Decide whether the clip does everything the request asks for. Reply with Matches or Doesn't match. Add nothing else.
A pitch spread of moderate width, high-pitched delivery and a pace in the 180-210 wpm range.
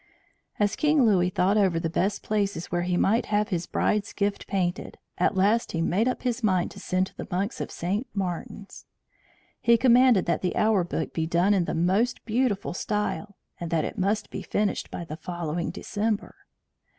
Matches